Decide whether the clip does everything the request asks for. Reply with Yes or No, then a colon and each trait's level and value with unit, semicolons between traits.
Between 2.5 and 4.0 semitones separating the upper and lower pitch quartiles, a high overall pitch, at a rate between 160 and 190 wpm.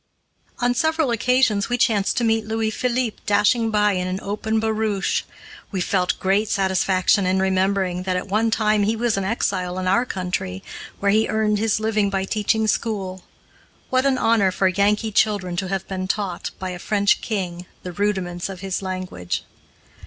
Yes: average, 2.8 semitones; high, 200 Hz; average, 175 wpm